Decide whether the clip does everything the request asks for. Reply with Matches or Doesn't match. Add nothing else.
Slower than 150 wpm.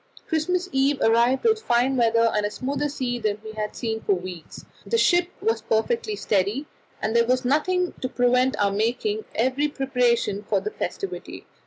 Doesn't match